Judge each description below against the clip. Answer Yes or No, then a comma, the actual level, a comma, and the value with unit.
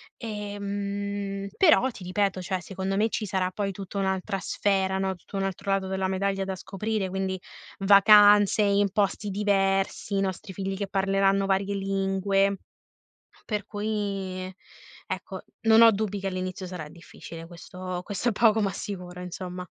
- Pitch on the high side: Yes, high, 195 Hz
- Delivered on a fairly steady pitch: Yes, narrow, 1.2 semitones